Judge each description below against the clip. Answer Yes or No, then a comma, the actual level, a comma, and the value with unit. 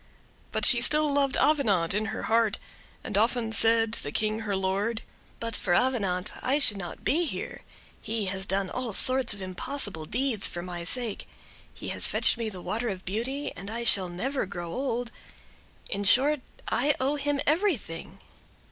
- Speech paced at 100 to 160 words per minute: No, average, 175 wpm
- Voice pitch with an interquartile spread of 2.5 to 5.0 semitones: No, wide, 5.4 semitones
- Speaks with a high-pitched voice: Yes, high, 225 Hz